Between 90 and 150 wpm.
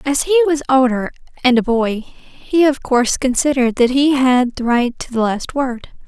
No: average, 200 wpm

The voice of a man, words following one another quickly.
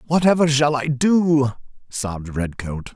No: male; slow, 120 wpm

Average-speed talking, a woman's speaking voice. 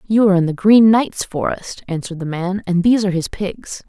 No: fast, 230 wpm; female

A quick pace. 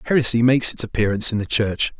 Yes: fast, 210 wpm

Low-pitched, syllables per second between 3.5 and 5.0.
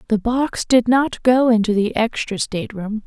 No: high, 230 Hz; 4.6 syllables/s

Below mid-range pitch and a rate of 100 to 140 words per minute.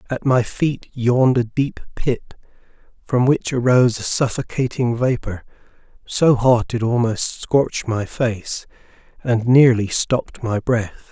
Yes: low, 120 Hz; slow, 135 wpm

